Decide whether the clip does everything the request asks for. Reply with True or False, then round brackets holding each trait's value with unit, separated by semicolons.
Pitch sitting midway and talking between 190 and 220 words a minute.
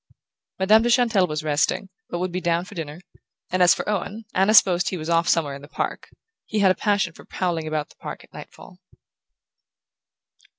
True (180 Hz; 200 wpm)